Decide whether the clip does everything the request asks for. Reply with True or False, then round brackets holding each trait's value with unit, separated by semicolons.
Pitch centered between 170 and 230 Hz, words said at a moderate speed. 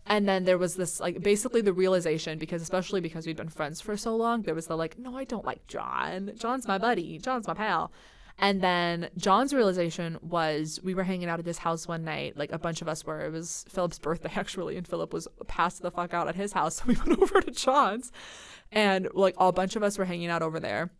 False (185 Hz; 245 wpm)